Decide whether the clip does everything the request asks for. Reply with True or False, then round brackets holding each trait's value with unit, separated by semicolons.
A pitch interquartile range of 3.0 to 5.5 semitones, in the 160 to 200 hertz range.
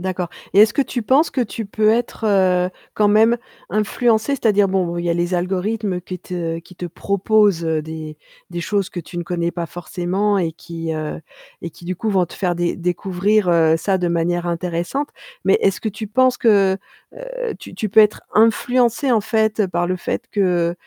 True (3.9 semitones; 190 Hz)